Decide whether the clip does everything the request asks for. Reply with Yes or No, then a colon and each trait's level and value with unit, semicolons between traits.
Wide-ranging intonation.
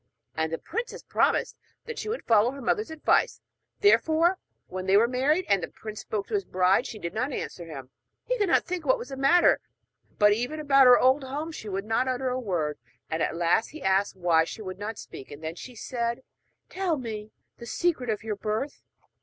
Yes: wide, 6.9 semitones